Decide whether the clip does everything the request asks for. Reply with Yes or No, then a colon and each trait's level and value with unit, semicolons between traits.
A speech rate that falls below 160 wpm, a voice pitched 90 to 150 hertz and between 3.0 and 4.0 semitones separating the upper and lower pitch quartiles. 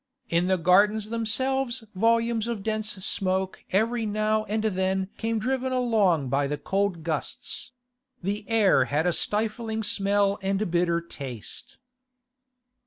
No: slow, 135 wpm; high, 205 Hz; average, 3.4 semitones